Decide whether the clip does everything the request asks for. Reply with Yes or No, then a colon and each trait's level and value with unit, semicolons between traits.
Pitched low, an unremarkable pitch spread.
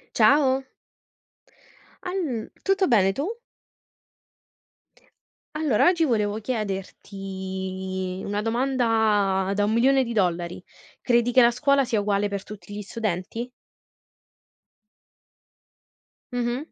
No: high, 220 Hz; average, 4.7 semitones